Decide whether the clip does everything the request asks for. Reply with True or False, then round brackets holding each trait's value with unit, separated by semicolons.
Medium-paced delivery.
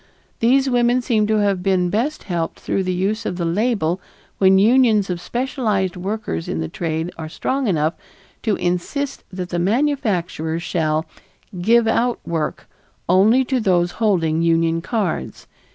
True (150 wpm)